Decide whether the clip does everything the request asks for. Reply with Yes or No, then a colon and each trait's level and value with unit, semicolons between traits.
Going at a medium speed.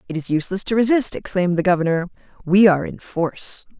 Yes: average, 190 wpm